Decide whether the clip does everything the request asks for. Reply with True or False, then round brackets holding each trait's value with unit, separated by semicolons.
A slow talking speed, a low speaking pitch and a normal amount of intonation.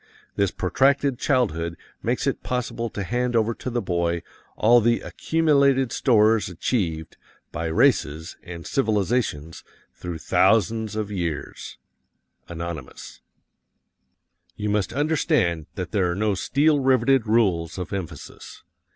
False (120 wpm; 105 Hz; 6.4 semitones)